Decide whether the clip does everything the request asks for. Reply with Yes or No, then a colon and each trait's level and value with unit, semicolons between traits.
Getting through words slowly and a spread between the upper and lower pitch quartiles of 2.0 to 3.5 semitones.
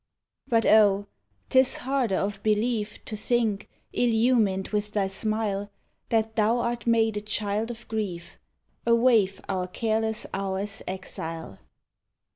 Yes: slow, 125 wpm; narrow, 2.6 semitones